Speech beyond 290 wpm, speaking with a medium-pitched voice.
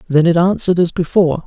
No: fast, 205 wpm; medium, 170 Hz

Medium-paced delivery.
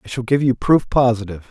No: fast, 240 wpm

